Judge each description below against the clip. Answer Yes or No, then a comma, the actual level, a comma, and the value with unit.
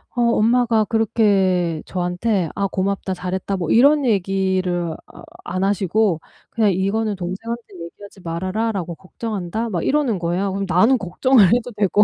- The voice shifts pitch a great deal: No, average, 3.6 semitones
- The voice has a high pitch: Yes, high, 195 Hz